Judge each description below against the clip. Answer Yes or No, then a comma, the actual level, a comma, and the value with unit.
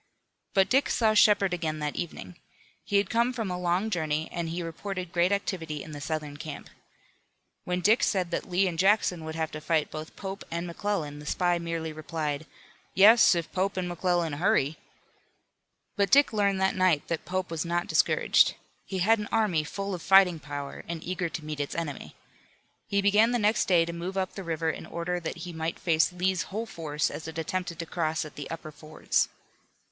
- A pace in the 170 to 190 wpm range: No, average, 200 wpm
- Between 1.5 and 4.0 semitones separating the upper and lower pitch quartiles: Yes, average, 3.3 semitones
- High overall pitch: No, medium, 175 Hz